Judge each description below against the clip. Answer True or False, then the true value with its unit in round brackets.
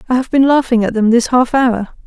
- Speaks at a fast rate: True (260 wpm)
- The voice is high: True (245 Hz)